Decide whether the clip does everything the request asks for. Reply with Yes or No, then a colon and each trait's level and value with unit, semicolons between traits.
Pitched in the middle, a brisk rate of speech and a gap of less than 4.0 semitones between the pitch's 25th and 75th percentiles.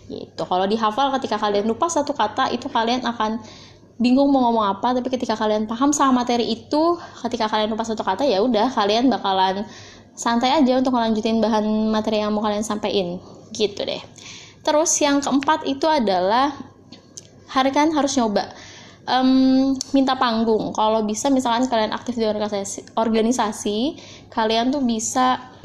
No: high, 230 Hz; fast, 150 wpm; average, 3.6 semitones